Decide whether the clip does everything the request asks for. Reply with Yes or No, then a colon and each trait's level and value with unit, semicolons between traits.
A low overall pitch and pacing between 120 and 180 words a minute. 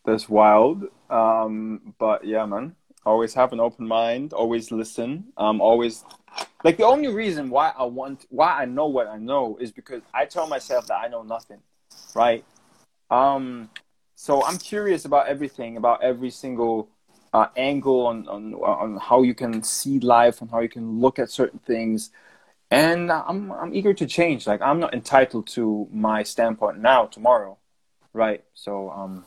Yes: low, 115 Hz; average, 170 wpm